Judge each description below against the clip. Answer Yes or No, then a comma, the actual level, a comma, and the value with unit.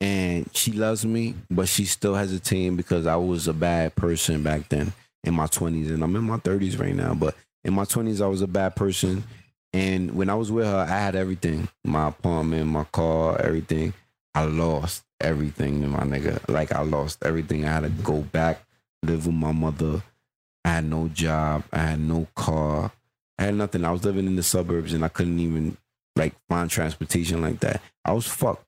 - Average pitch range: Yes, average, 3.3 semitones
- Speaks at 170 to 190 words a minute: No, fast, 205 wpm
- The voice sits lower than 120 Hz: Yes, very low, 85 Hz